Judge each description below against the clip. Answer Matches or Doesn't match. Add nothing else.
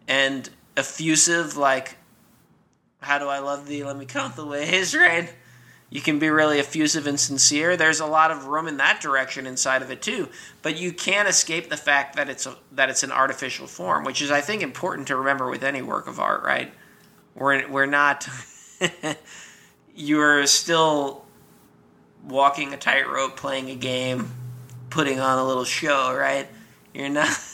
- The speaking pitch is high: Doesn't match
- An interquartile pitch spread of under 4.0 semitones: Matches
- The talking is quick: Doesn't match